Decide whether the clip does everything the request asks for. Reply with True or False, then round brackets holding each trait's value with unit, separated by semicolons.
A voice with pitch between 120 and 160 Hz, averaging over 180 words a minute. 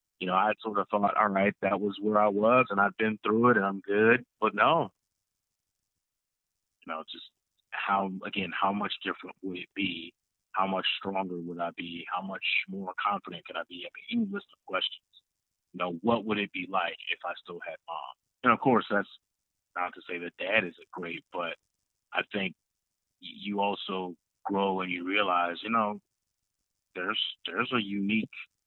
False (100 Hz; 190 wpm)